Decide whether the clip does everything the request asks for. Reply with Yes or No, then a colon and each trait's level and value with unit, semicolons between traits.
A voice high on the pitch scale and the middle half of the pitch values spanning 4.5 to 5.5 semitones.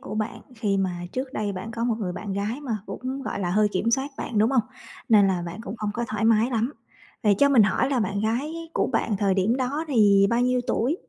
No: high, 220 Hz; average, 3.9 semitones